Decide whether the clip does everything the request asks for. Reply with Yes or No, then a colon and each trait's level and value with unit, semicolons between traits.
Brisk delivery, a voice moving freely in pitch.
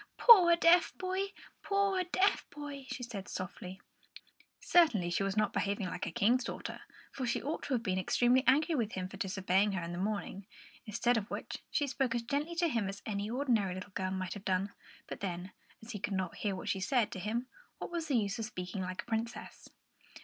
Yes: fast, 215 wpm; wide, 6.2 semitones